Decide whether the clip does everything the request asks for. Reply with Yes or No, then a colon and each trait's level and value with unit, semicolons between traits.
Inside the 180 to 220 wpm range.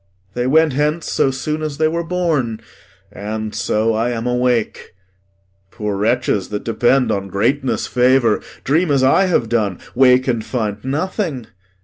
No: average, 150 wpm